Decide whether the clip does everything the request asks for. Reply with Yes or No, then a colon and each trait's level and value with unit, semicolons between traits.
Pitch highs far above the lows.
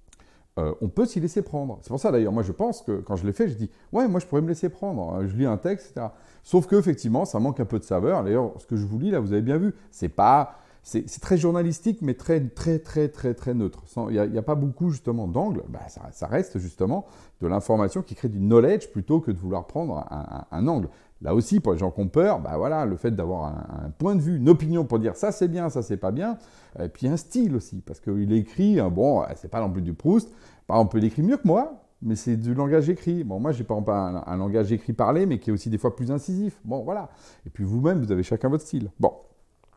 Yes: wide, 8.7 semitones